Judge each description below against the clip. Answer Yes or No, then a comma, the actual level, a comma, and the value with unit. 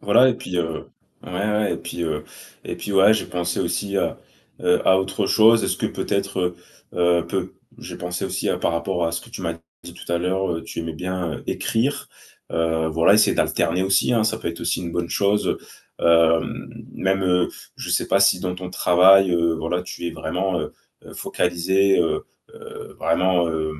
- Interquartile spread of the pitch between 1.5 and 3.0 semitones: Yes, narrow, 2.5 semitones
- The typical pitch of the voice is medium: No, very low, 90 Hz